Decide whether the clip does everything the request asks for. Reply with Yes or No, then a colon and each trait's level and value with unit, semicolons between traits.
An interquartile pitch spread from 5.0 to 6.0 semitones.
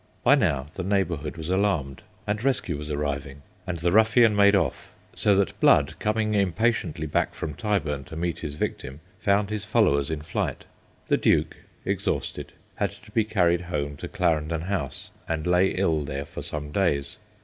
Yes: wide, 5.4 semitones